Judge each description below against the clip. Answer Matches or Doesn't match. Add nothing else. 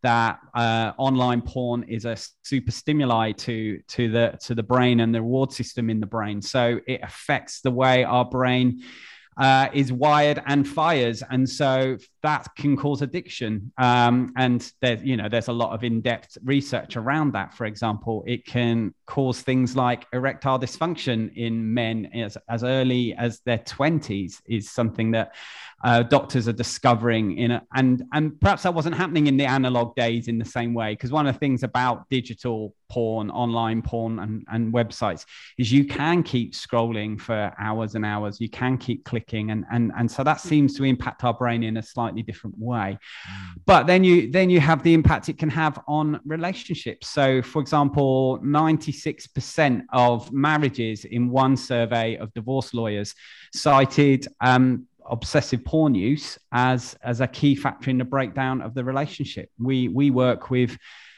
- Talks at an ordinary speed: Matches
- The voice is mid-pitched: Doesn't match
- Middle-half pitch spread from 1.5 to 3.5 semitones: Matches